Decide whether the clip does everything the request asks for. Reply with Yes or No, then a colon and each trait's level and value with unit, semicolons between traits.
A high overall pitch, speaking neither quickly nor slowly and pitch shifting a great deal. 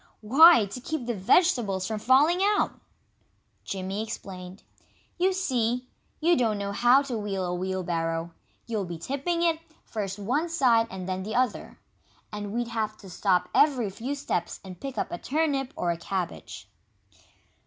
Yes: high, 220 Hz; average, 160 wpm; wide, 6.3 semitones